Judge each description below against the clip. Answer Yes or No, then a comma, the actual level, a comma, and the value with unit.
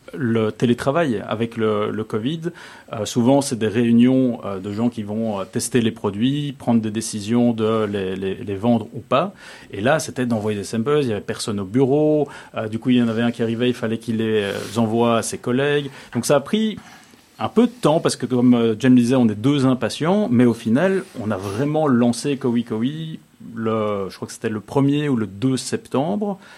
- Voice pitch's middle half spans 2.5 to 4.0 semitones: Yes, average, 3.7 semitones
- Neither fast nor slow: No, fast, 225 wpm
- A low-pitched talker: Yes, low, 120 Hz